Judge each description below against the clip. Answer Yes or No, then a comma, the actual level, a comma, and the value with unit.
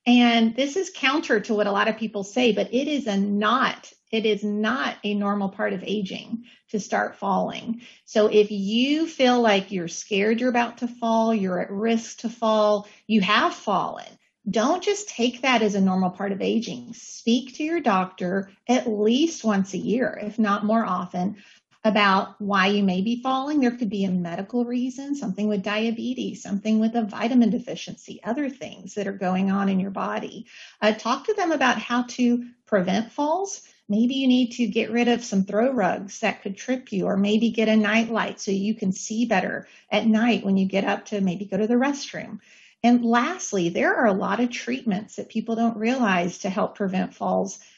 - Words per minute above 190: Yes, average, 200 wpm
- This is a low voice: No, high, 220 Hz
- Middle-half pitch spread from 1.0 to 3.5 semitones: Yes, average, 3.0 semitones